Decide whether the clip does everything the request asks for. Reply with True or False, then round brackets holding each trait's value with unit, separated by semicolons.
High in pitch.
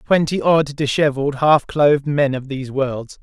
False (140 Hz)